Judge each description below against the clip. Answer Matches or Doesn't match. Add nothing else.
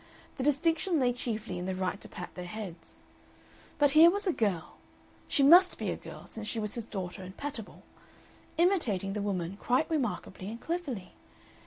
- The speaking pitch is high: Matches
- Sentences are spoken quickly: Doesn't match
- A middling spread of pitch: Doesn't match